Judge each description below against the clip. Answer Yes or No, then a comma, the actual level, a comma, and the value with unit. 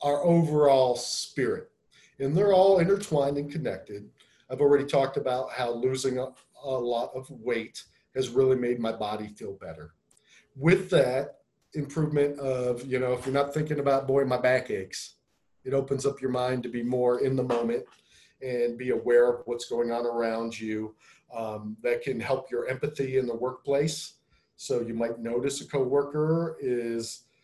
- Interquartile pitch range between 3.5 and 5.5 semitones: No, average, 2.8 semitones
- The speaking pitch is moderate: No, low, 130 Hz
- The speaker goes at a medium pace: Yes, average, 170 wpm